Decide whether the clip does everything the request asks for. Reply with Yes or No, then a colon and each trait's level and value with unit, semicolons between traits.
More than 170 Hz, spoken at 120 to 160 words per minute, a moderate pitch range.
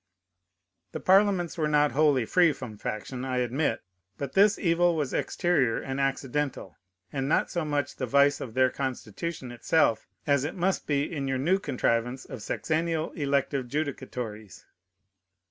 No: medium, 140 Hz; average, 150 wpm; average, 3.8 semitones